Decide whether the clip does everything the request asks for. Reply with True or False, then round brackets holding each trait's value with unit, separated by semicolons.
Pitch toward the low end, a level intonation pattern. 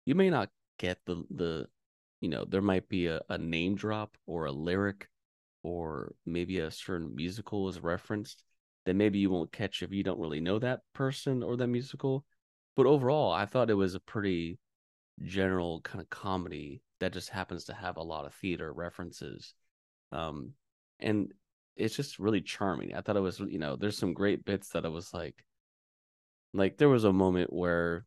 False (95 Hz; 3.6 semitones)